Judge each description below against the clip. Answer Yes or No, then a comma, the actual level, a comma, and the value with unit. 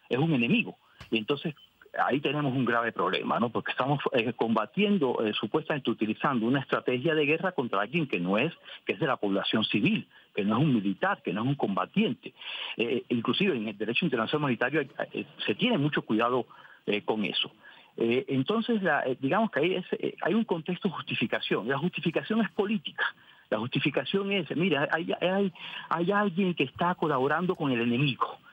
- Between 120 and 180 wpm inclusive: No, fast, 190 wpm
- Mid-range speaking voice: Yes, medium, 155 Hz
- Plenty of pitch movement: Yes, wide, 6.6 semitones